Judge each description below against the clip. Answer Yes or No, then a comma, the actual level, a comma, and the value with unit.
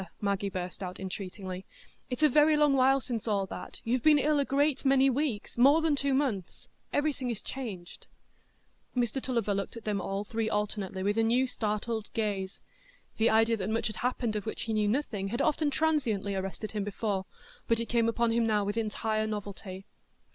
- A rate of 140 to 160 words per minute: No, average, 185 wpm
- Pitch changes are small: No, average, 4.4 semitones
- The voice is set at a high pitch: Yes, high, 225 Hz